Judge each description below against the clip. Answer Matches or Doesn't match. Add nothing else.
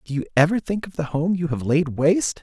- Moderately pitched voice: Matches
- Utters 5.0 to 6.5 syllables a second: Matches